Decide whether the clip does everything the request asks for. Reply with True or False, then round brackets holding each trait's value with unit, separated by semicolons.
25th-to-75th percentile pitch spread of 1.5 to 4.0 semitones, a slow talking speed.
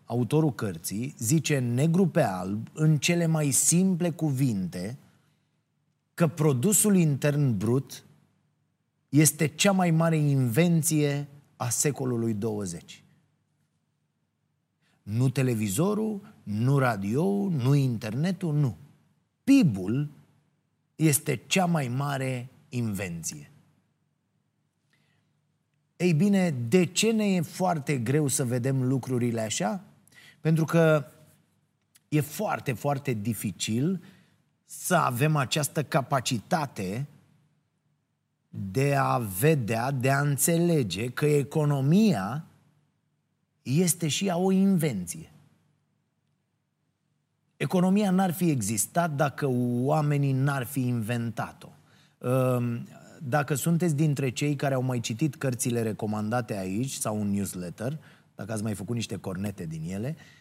False (4.4 semitones; 100 wpm)